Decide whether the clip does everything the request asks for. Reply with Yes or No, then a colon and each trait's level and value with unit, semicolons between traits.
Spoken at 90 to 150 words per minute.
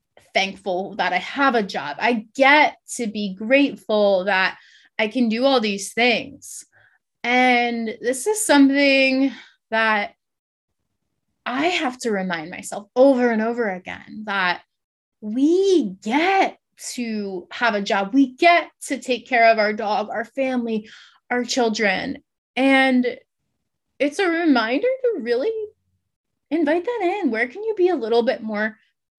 Yes: average, 140 wpm